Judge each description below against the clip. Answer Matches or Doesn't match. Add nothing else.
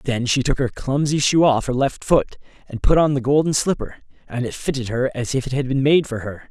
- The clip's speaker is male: Matches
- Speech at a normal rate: Doesn't match